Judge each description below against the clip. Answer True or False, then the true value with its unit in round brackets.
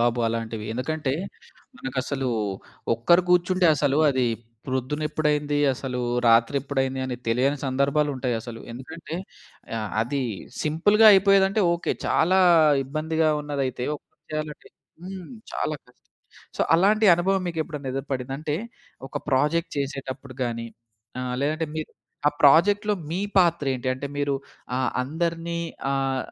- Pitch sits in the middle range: True (145 Hz)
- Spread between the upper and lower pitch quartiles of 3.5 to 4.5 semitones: True (4.2 semitones)